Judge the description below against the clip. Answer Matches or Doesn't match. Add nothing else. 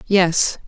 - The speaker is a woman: Matches